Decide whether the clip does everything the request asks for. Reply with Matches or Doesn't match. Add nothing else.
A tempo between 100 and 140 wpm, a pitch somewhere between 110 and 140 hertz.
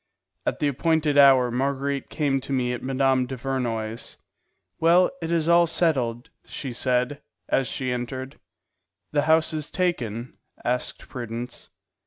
Matches